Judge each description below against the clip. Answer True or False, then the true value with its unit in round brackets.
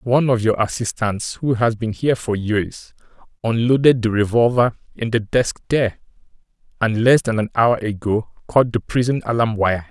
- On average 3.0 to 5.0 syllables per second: True (4.9 syllables/s)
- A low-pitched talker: True (115 Hz)